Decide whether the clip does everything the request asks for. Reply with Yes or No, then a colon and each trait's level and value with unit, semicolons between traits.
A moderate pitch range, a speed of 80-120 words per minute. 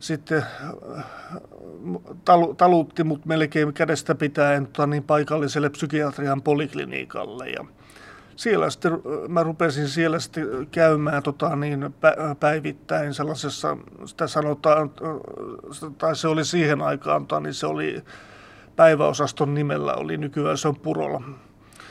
No: narrow, 1.7 semitones; average, 105 wpm